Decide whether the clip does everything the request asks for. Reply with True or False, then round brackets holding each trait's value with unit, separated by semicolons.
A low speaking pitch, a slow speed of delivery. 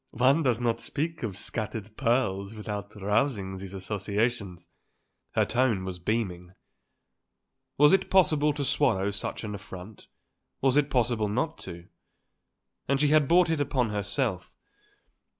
True (110 Hz; 130 wpm)